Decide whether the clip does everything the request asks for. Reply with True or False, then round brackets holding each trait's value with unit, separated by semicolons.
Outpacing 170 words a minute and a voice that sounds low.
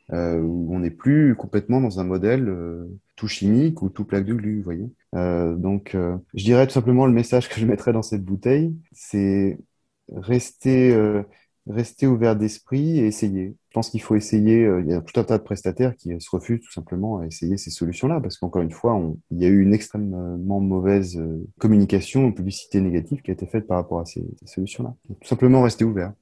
True (215 wpm; 105 Hz)